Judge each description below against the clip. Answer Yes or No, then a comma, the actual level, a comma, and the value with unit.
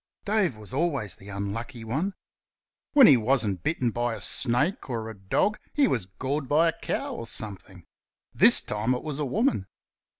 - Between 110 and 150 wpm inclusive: No, average, 175 wpm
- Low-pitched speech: Yes, low, 120 Hz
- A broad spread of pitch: Yes, wide, 6.3 semitones